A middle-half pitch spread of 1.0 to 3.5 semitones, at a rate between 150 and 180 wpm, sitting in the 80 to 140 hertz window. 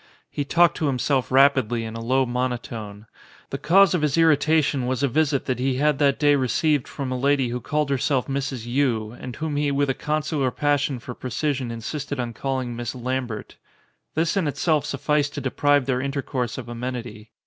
No: average, 2.9 semitones; average, 190 wpm; low, 135 Hz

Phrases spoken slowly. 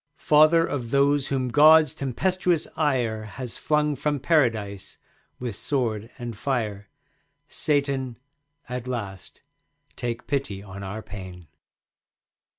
Yes: slow, 110 wpm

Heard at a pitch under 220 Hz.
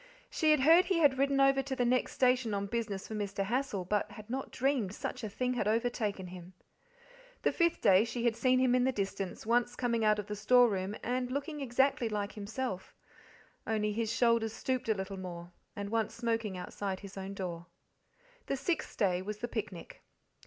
No: high, 225 Hz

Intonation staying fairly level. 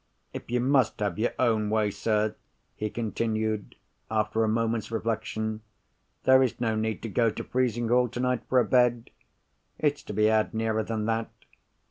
Yes: narrow, 1.8 semitones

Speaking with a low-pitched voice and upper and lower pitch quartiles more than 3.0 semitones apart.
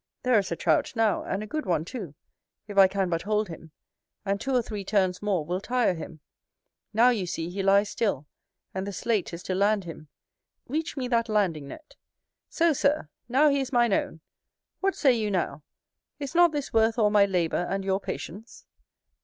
No: high, 205 Hz; average, 4.7 semitones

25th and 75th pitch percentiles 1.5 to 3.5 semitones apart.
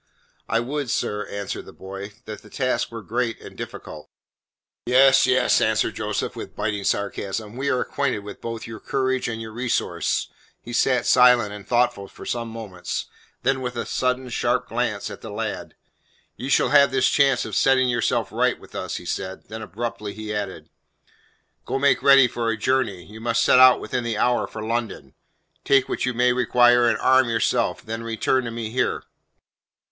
Yes: average, 2.8 semitones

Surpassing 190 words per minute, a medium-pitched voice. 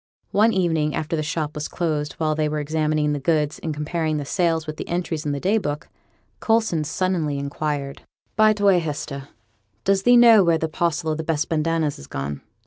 Yes: average, 200 wpm; medium, 155 Hz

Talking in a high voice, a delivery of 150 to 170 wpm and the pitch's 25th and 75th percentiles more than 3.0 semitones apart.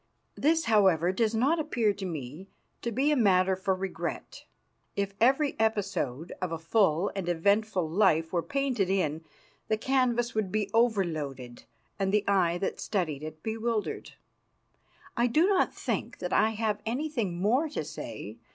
Yes: high, 200 Hz; average, 155 wpm; average, 4.9 semitones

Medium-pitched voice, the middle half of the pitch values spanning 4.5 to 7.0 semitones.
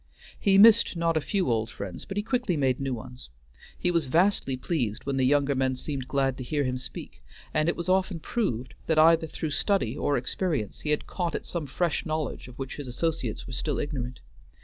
Yes: medium, 145 Hz; average, 4.9 semitones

